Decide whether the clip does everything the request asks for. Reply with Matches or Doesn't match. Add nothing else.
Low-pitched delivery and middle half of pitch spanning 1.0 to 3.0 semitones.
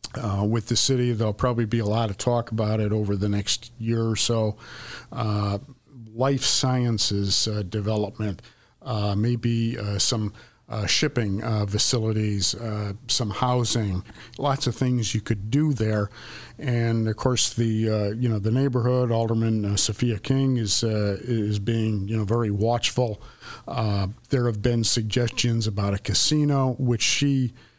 Matches